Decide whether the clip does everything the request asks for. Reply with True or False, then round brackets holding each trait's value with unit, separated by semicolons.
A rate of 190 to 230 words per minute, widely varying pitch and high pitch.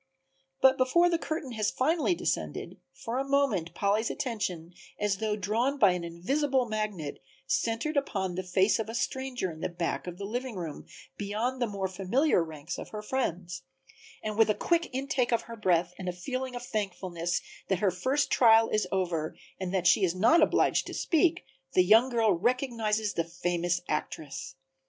False (180 wpm; 6.1 semitones; 210 Hz)